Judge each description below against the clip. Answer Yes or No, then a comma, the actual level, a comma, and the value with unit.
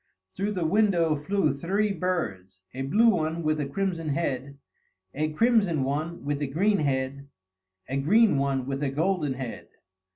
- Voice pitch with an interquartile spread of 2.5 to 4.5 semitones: No, average, 5.3 semitones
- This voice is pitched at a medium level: Yes, medium, 155 Hz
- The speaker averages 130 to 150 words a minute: No, average, 160 wpm